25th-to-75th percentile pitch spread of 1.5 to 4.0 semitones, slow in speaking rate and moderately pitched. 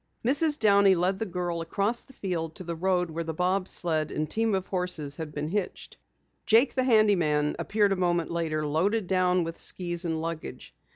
No: average, 3.4 semitones; average, 195 wpm; medium, 180 Hz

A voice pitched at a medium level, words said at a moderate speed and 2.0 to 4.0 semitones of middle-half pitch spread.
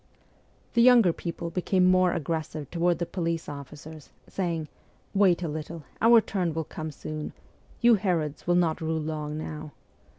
Yes: medium, 165 Hz; average, 160 wpm; average, 2.8 semitones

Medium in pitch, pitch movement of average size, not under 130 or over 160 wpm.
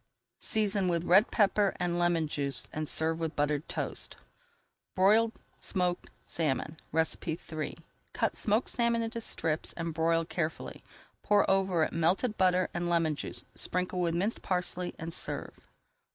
Yes: medium, 175 Hz; average, 3.1 semitones; average, 140 wpm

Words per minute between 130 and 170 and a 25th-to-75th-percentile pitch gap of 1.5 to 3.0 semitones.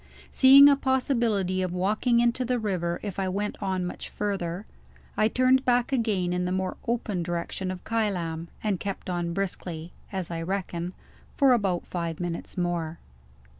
No: average, 165 wpm; average, 4.6 semitones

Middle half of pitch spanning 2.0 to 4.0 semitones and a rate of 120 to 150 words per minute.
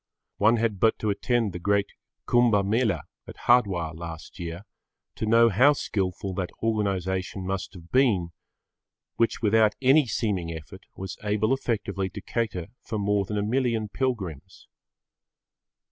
Yes: average, 3.7 semitones; average, 145 wpm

